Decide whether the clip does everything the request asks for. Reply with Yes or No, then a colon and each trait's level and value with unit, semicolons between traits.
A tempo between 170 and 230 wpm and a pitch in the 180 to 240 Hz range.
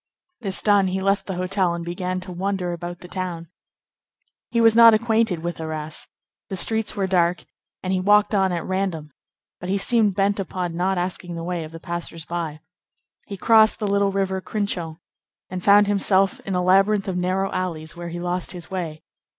Yes: average, 190 wpm; medium, 185 Hz